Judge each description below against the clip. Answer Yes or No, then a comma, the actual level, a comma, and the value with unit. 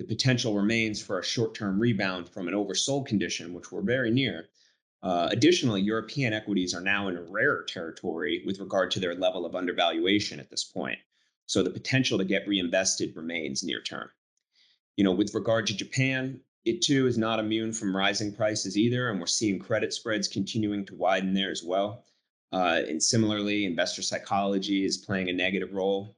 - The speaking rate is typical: Yes, average, 185 wpm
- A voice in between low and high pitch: No, low, 100 Hz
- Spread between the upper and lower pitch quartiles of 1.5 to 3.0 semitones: Yes, narrow, 2.6 semitones